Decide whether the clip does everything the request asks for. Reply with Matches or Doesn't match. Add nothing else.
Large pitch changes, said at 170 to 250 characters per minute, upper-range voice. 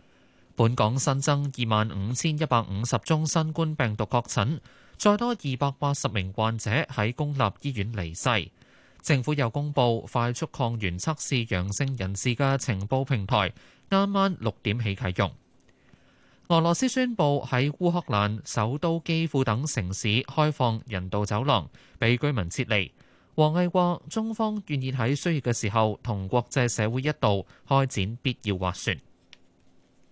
Doesn't match